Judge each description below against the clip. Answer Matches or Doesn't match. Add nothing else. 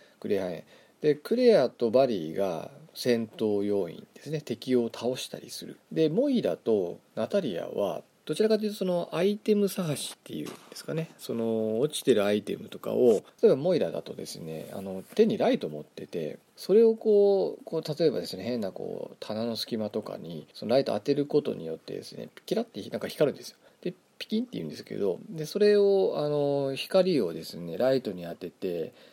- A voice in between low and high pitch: Matches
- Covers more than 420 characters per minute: Doesn't match